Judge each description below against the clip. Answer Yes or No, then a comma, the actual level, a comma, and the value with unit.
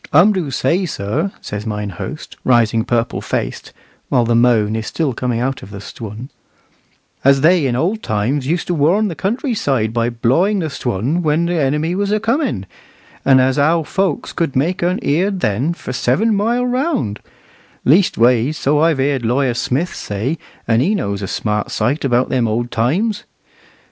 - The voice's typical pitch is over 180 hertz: No, low, 135 Hz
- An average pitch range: No, wide, 7.0 semitones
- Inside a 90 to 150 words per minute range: No, average, 180 wpm